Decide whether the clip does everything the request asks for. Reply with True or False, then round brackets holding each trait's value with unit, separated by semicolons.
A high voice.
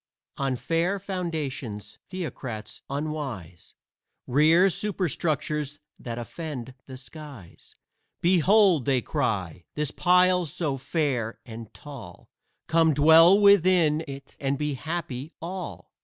False (150 Hz)